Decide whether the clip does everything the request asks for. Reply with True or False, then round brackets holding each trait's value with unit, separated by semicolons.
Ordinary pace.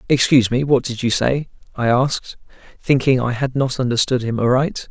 True (185 wpm)